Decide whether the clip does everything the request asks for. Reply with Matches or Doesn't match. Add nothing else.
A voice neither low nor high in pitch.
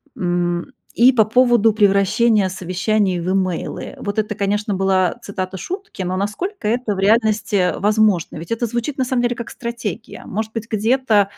Doesn't match